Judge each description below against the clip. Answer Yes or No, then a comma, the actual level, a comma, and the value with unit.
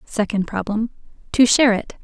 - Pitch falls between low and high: No, high, 220 Hz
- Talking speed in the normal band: Yes, average, 145 wpm